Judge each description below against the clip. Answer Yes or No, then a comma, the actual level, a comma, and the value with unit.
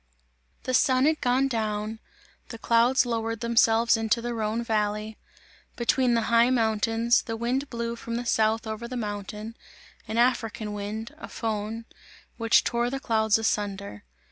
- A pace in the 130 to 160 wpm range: Yes, average, 150 wpm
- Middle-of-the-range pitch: No, high, 230 Hz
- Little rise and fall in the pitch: Yes, narrow, 1.5 semitones